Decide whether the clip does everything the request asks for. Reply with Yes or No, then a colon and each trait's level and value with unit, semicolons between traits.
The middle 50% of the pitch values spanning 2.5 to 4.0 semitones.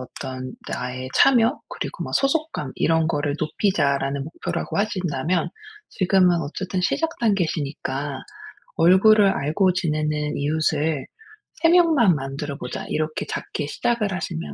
No: wide, 5.4 semitones